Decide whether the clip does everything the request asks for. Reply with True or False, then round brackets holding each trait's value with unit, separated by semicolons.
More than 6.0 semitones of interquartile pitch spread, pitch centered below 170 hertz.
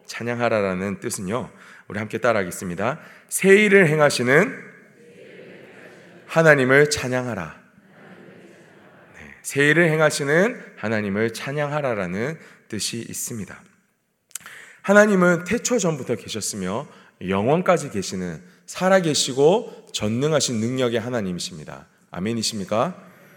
True (7.7 semitones; 140 Hz)